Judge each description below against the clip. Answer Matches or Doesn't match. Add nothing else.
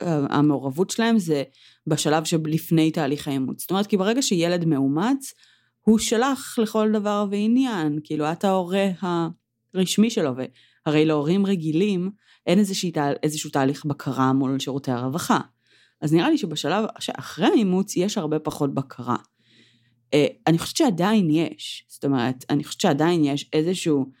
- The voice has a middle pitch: Matches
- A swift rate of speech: Doesn't match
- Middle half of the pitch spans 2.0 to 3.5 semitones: Doesn't match